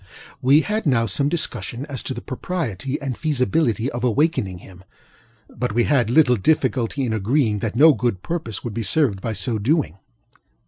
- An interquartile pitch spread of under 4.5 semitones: No, average, 4.9 semitones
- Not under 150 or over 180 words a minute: Yes, average, 175 wpm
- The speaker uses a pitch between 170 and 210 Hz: No, low, 125 Hz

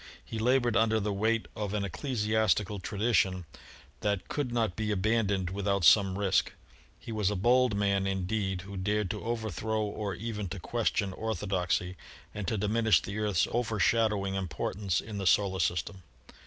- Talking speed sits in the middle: Yes, average, 155 wpm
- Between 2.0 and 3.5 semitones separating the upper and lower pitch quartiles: Yes, narrow, 2.4 semitones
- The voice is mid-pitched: No, low, 105 Hz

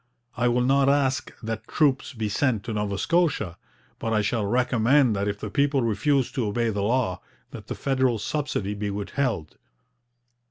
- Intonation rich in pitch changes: No, average, 4.5 semitones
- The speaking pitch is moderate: No, low, 120 Hz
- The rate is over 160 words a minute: Yes, average, 170 wpm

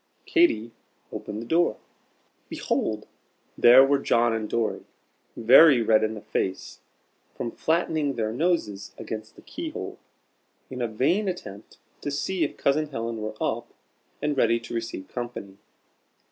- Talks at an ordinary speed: Yes, average, 145 wpm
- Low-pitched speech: Yes, low, 120 Hz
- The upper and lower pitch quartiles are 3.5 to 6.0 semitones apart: Yes, average, 5.3 semitones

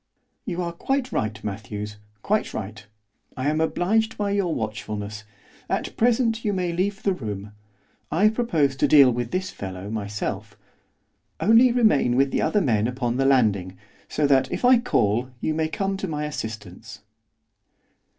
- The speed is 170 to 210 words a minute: No, average, 160 wpm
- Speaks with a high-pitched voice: No, medium, 140 Hz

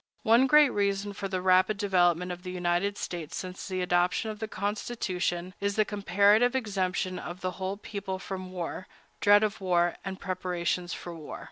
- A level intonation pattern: Yes, narrow, 2.2 semitones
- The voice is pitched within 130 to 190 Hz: Yes, medium, 185 Hz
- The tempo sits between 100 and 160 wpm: No, average, 175 wpm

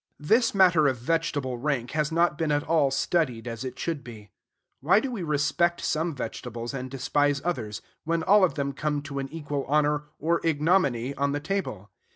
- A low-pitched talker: No, medium, 145 Hz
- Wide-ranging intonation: No, average, 3.8 semitones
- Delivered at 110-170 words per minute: No, average, 190 wpm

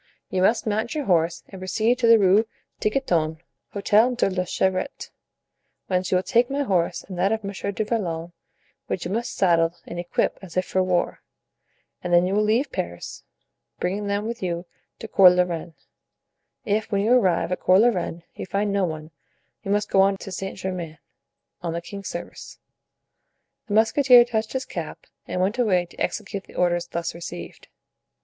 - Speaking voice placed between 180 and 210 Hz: Yes, high, 190 Hz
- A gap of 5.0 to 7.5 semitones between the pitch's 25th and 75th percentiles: No, average, 3.6 semitones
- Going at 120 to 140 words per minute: No, average, 185 wpm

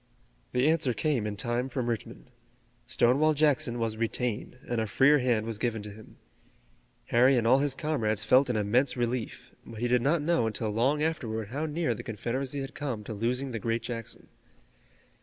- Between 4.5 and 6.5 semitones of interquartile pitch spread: No, average, 3.5 semitones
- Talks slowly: No, average, 185 wpm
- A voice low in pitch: Yes, low, 120 Hz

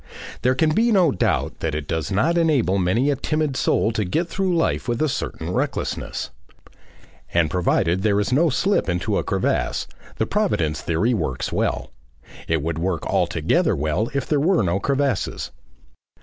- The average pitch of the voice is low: Yes, low, 110 Hz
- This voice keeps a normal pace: Yes, average, 165 wpm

